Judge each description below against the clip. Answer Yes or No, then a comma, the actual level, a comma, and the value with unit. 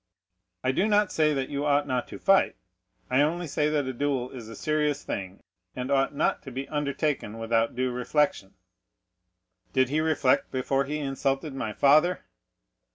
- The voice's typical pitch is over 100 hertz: Yes, medium, 140 Hz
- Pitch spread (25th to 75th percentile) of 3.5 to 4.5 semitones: No, average, 2.7 semitones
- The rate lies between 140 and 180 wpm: Yes, average, 170 wpm